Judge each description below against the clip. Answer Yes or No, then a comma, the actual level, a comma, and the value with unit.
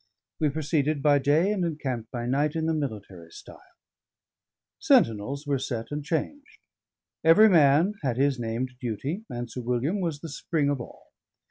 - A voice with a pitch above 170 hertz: No, medium, 145 Hz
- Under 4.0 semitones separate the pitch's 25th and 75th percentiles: No, average, 4.5 semitones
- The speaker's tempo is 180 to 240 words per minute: No, average, 160 wpm